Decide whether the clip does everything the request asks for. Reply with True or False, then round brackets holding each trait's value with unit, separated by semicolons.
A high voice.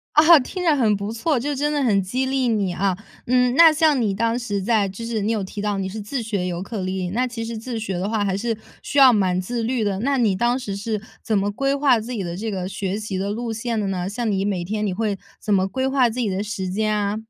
True (215 Hz)